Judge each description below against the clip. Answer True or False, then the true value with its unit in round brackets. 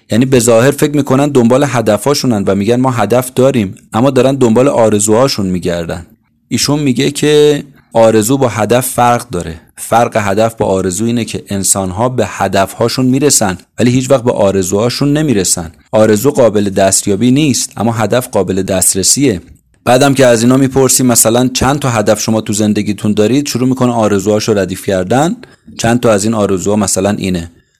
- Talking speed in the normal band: False (165 wpm)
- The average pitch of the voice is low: True (115 Hz)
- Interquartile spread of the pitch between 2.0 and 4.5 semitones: True (4.0 semitones)